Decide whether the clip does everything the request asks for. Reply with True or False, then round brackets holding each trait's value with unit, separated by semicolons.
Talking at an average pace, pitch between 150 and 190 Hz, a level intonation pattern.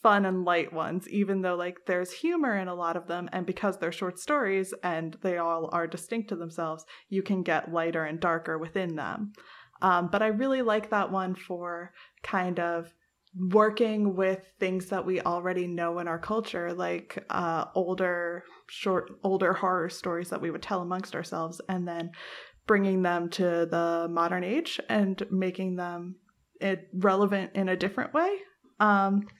True (175 wpm; 185 Hz; 2.3 semitones)